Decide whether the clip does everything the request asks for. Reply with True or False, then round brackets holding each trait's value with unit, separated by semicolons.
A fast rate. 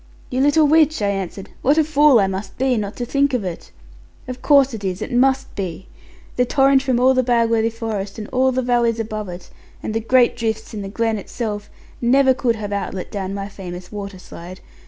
True (210 wpm)